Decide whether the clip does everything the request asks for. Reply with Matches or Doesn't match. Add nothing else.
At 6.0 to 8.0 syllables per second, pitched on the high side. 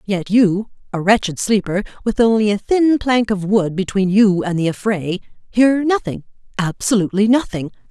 Doesn't match